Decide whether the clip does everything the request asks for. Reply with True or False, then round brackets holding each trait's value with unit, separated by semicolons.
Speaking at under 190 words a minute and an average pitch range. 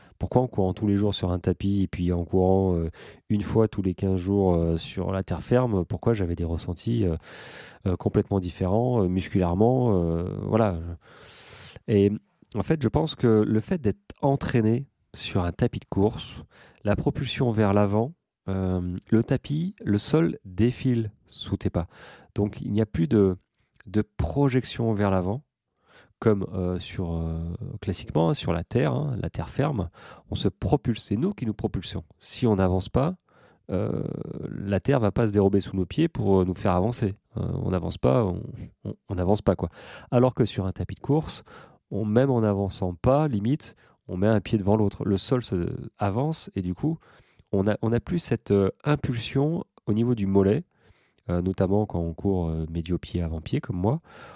True (180 wpm; 4.4 semitones)